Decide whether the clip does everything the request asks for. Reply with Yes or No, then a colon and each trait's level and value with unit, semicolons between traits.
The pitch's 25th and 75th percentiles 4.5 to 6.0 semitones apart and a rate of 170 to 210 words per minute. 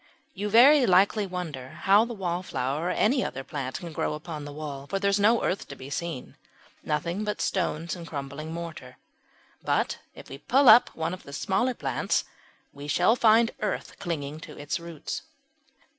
Yes: wide, 5.6 semitones; average, 180 wpm